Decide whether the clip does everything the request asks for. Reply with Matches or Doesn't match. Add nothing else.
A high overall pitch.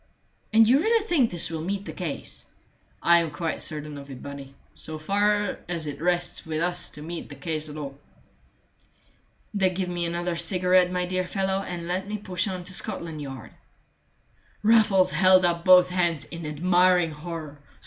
Doesn't match